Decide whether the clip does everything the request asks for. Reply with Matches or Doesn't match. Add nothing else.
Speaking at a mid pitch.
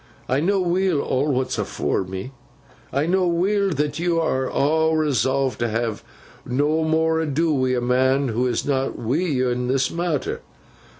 Matches